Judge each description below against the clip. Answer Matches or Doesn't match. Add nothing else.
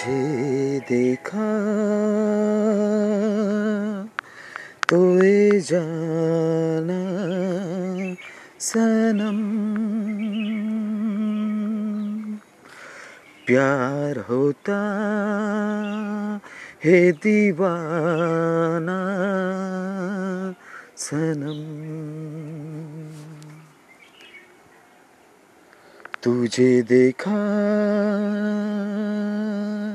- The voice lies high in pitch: Matches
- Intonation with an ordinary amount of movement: Matches